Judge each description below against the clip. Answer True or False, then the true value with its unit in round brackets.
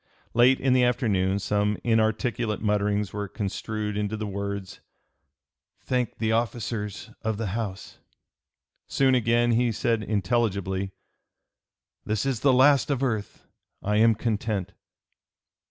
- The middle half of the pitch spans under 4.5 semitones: True (2.6 semitones)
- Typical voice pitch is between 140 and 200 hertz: False (110 Hz)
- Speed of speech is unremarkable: False (120 wpm)